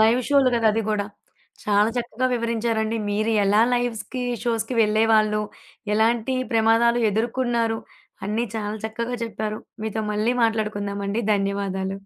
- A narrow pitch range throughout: Yes, narrow, 1.7 semitones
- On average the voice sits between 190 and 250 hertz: Yes, high, 220 Hz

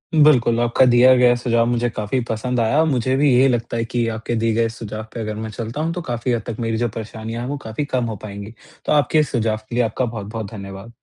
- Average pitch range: No, narrow, 2.1 semitones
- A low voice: Yes, low, 115 Hz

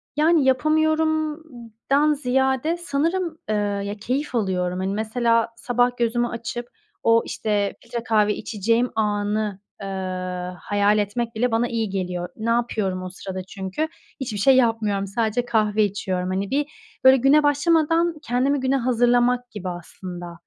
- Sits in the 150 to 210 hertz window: No, high, 230 Hz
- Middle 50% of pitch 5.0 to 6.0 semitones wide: No, average, 4.5 semitones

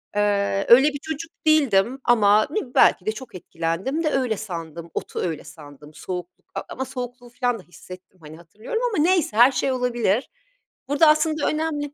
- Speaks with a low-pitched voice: No, high, 240 Hz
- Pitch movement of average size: No, wide, 7.6 semitones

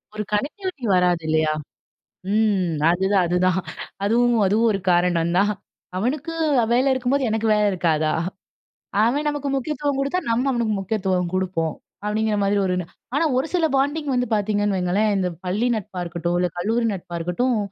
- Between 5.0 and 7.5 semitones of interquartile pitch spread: Yes, wide, 5.6 semitones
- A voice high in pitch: Yes, high, 210 Hz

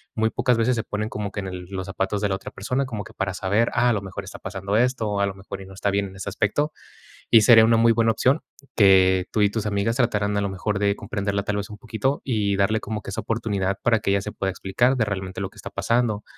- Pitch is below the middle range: Yes, low, 105 Hz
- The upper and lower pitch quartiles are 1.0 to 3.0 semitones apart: Yes, narrow, 2.6 semitones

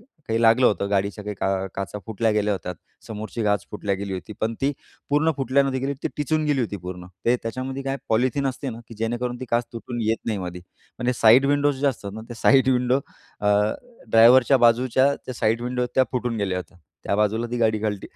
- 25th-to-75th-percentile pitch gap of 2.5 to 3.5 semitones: No, average, 3.9 semitones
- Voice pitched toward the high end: No, low, 115 Hz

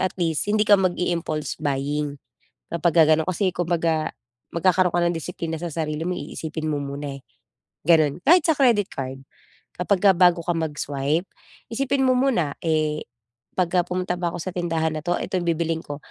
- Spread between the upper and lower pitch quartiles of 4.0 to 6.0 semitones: No, average, 2.8 semitones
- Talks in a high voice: No, medium, 170 Hz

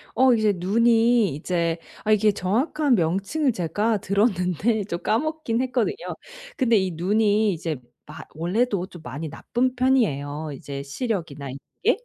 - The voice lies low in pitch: No, high, 205 Hz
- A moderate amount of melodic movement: No, wide, 5.9 semitones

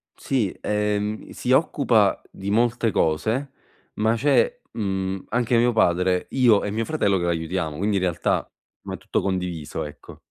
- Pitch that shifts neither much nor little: Yes, average, 4.1 semitones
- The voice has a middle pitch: No, low, 105 Hz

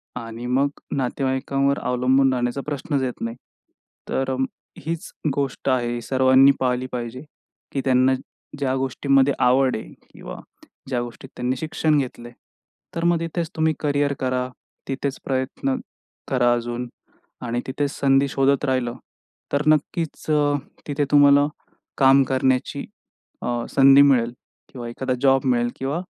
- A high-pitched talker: No, low, 135 Hz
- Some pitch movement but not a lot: No, narrow, 2.0 semitones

